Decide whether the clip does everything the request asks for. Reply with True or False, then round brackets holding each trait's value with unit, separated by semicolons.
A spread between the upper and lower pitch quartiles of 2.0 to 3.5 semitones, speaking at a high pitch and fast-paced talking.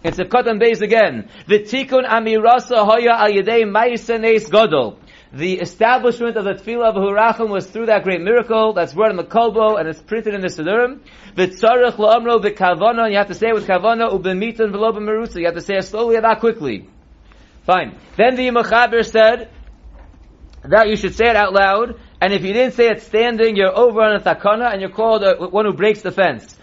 True (2.8 semitones; 220 Hz; 215 wpm)